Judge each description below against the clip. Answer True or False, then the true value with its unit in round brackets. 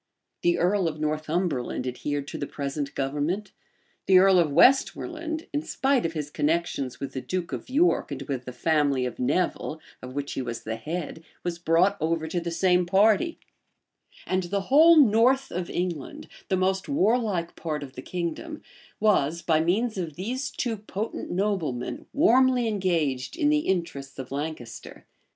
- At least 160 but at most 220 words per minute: True (165 wpm)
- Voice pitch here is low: False (175 Hz)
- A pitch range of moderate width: False (6.3 semitones)